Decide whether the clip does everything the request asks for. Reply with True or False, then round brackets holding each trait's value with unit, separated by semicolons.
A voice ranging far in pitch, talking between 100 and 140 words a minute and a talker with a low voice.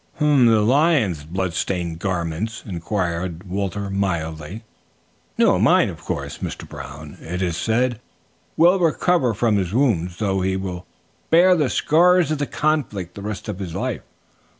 False (6.5 semitones; 150 wpm; 100 Hz)